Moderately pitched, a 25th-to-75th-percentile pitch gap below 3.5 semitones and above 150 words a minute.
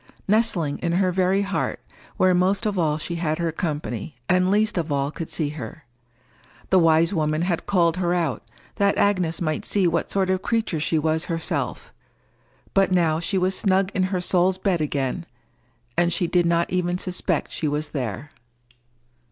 Yes: medium, 175 Hz; average, 3.0 semitones; average, 175 wpm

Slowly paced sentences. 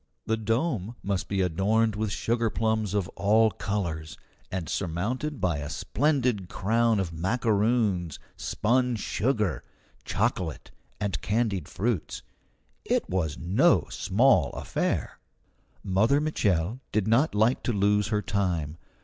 Yes: slow, 120 wpm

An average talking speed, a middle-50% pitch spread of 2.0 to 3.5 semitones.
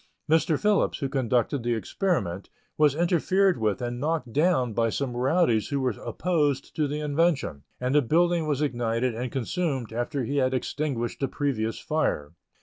No: average, 165 wpm; average, 4.5 semitones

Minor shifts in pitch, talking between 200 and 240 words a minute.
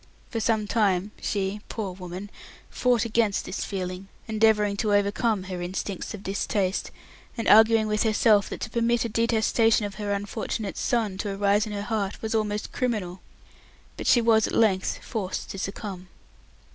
No: narrow, 2.2 semitones; average, 165 wpm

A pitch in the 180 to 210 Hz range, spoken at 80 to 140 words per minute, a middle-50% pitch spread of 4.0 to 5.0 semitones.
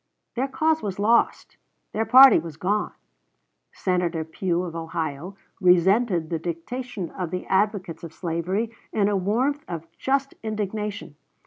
Yes: high, 190 Hz; slow, 135 wpm; average, 4.7 semitones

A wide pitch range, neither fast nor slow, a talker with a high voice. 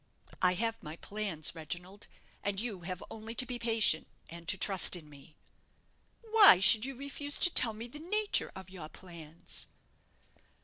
Yes: wide, 5.7 semitones; average, 170 wpm; high, 200 Hz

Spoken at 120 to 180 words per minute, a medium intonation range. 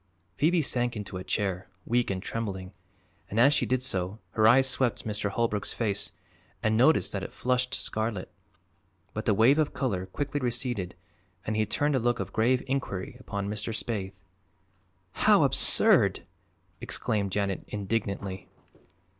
Yes: average, 150 wpm; average, 4.1 semitones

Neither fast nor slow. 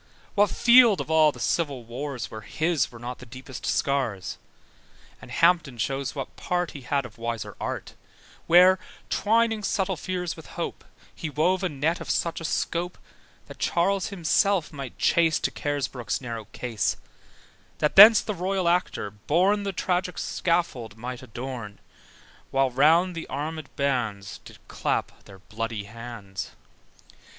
Yes: average, 150 wpm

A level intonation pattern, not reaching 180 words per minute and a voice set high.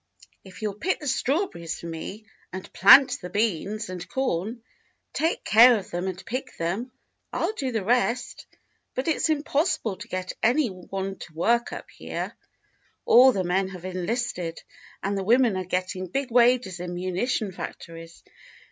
No: average, 5.3 semitones; average, 165 wpm; high, 200 Hz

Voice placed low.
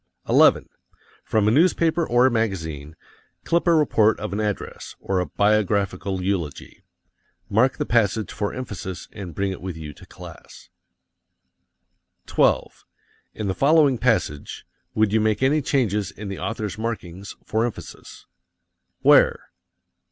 Yes: low, 105 Hz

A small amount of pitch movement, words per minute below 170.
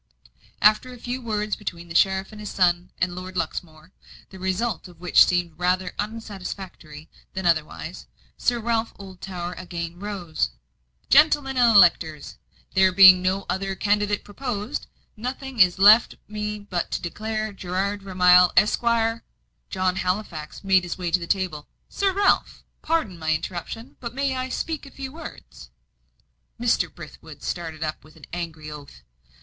No: average, 4.0 semitones; average, 150 wpm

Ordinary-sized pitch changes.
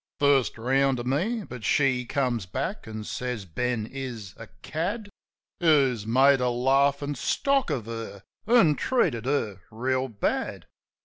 Yes: average, 3.5 semitones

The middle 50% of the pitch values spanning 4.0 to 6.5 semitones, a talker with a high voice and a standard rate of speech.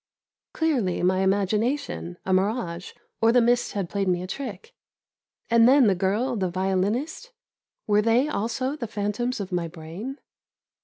Yes: average, 4.7 semitones; high, 210 Hz; average, 150 wpm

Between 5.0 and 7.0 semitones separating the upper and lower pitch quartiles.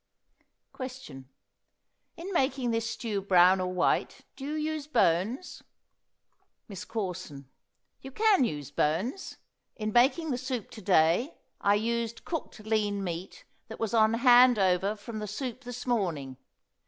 Yes: wide, 5.5 semitones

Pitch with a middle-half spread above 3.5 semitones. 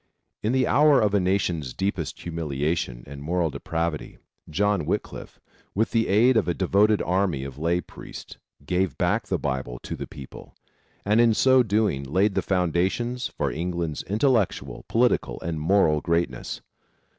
Yes: average, 5.2 semitones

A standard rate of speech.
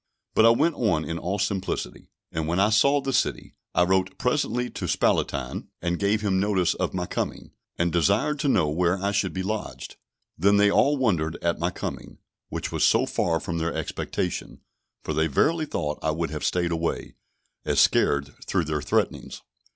Yes: average, 190 wpm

